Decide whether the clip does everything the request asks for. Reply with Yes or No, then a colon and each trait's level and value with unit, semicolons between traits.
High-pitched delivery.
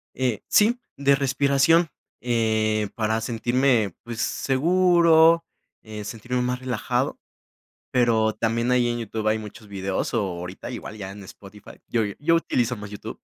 No: low, 120 Hz